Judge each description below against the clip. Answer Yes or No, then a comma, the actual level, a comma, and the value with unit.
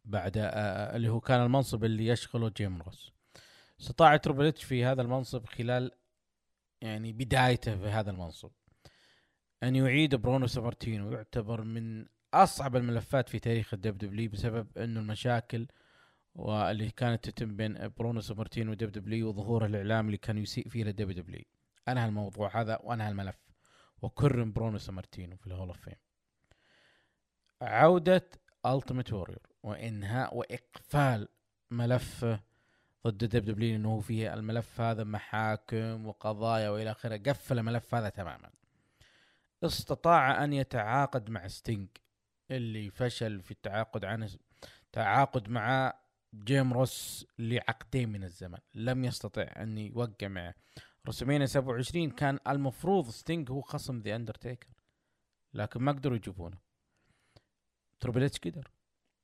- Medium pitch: No, low, 115 Hz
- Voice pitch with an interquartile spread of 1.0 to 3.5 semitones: Yes, average, 2.9 semitones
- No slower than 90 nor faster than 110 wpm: No, average, 125 wpm